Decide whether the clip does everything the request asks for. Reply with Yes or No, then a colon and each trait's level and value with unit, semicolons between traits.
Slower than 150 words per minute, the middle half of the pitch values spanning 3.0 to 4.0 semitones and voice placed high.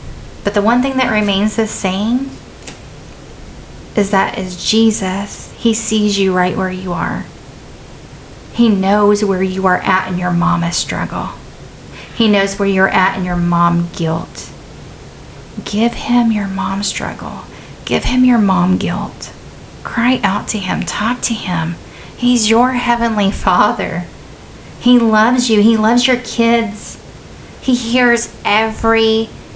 Yes: average, 140 wpm; average, 3.6 semitones; high, 210 Hz